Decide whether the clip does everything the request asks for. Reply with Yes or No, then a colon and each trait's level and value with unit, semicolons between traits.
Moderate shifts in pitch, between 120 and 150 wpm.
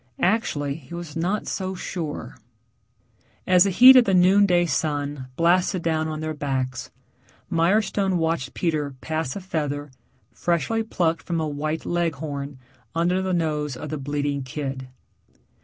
Yes: average, 3.7 semitones; average, 145 wpm